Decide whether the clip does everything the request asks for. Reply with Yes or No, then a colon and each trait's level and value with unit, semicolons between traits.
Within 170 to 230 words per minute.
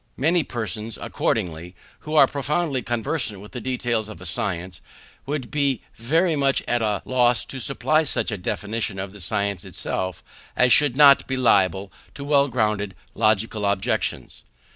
No: average, 160 wpm